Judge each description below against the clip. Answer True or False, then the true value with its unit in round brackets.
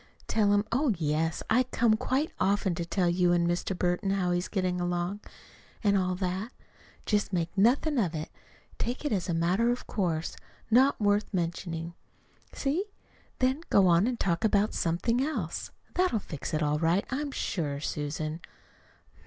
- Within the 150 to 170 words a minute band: True (165 wpm)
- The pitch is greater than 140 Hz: True (190 Hz)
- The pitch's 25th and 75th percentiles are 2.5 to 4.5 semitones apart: False (4.9 semitones)